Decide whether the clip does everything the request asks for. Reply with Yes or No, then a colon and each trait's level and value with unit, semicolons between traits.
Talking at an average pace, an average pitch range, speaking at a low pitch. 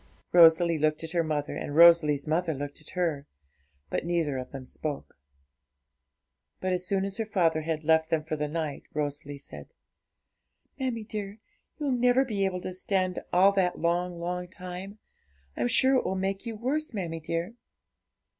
No: average, 170 wpm; average, 3.9 semitones; medium, 175 Hz